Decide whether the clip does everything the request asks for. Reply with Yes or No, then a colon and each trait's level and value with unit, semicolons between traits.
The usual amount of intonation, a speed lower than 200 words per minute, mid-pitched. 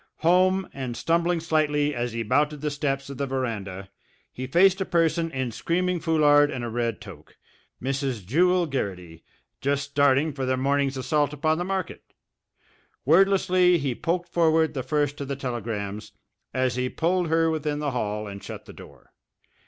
Yes: average, 4.5 semitones; average, 170 wpm; medium, 145 Hz